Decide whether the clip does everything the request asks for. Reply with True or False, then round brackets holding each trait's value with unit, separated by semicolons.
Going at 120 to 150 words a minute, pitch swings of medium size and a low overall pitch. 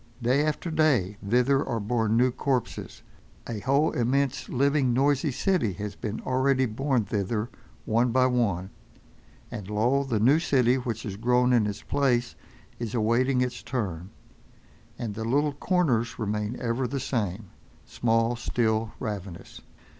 True (140 wpm; 3.5 semitones; 120 Hz)